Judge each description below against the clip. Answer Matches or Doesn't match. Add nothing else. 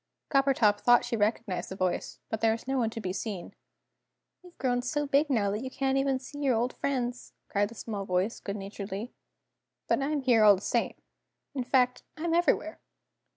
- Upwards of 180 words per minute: Matches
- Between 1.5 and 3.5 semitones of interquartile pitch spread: Doesn't match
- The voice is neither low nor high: Doesn't match